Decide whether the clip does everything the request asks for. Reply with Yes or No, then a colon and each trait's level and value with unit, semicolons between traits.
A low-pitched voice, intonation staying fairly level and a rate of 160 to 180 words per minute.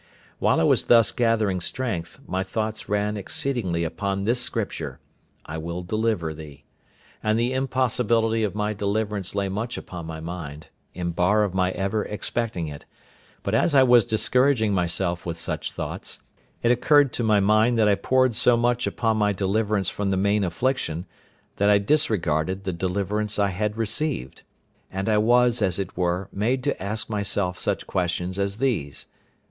No: low, 105 Hz; average, 3.8 semitones; average, 170 wpm